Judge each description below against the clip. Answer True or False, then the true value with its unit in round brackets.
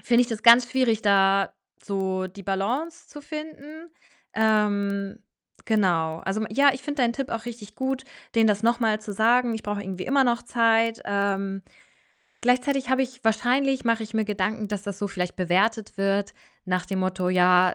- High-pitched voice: True (220 Hz)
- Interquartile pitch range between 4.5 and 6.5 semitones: False (3.8 semitones)